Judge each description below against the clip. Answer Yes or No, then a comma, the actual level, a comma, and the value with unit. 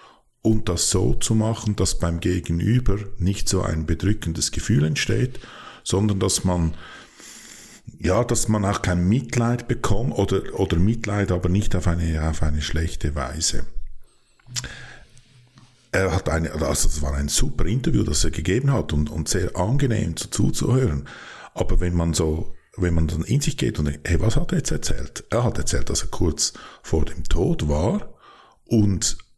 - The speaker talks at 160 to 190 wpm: Yes, average, 170 wpm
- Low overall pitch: Yes, very low, 90 Hz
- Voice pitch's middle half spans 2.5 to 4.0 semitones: No, wide, 5.5 semitones